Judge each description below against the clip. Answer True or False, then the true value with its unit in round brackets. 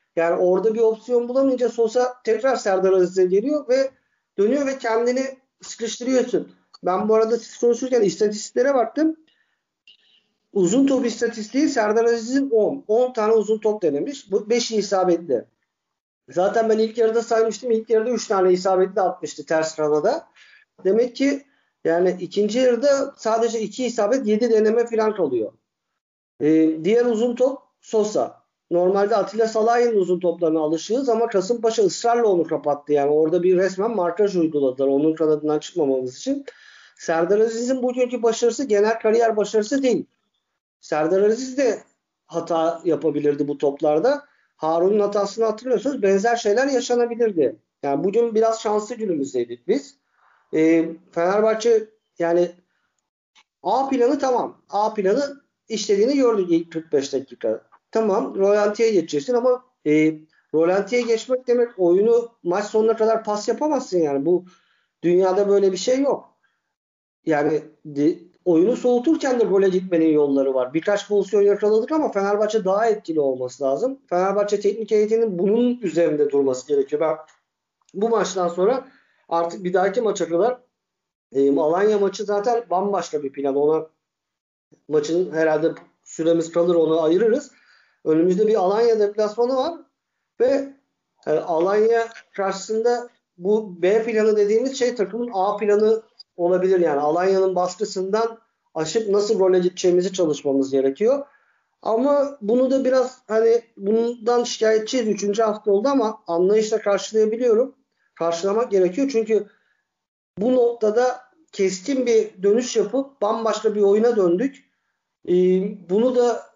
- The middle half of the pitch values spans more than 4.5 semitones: True (5.1 semitones)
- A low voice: False (215 Hz)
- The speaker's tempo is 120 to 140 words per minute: True (130 wpm)